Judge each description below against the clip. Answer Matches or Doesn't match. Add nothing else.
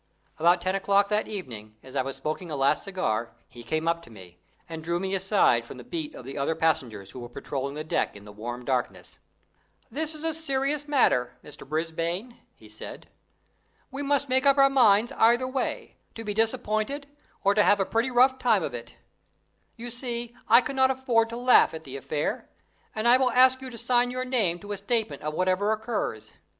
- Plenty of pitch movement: Matches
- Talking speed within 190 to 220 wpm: Matches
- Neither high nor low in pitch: Doesn't match